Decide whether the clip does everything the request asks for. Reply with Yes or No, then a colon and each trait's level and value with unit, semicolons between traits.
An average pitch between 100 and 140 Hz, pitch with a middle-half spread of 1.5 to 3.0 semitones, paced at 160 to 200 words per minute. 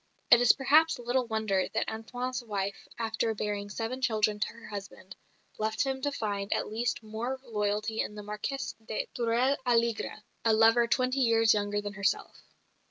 No: high, 225 Hz; average, 2.7 semitones; average, 165 wpm